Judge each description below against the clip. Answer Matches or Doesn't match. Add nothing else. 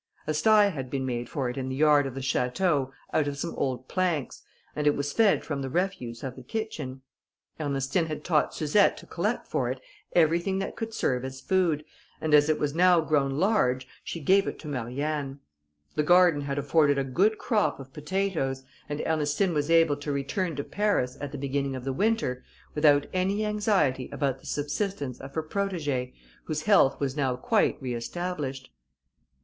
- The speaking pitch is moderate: Matches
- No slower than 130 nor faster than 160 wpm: Doesn't match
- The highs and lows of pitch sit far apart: Doesn't match